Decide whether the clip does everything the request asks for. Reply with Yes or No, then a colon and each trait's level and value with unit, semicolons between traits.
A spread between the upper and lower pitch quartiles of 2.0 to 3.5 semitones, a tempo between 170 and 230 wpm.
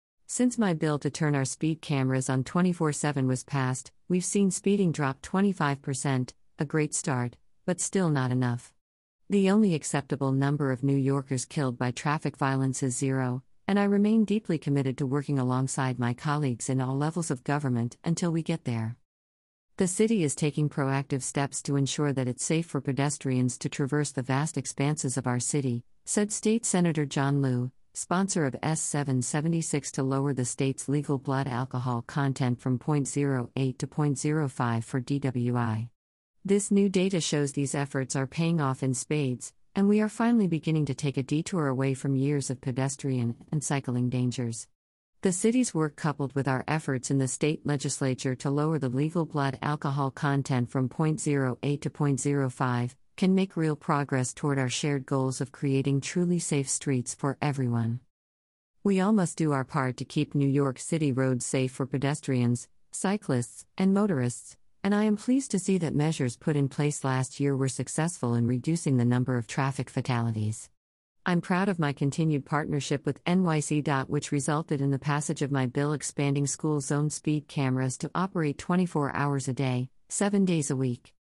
Yes: average, 3.0 semitones; average, 175 wpm